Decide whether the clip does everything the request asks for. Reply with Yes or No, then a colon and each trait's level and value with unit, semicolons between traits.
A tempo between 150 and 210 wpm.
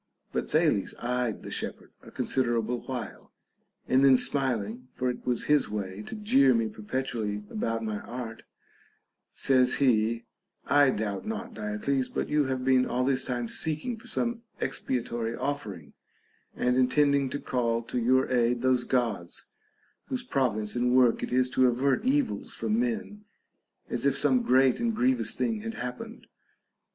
Yes: average, 155 wpm